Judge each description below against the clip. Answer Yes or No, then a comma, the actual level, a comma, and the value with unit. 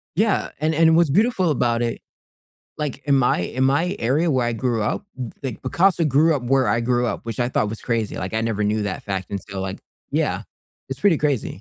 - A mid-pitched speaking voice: No, low, 125 Hz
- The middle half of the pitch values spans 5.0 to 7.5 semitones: Yes, wide, 5.5 semitones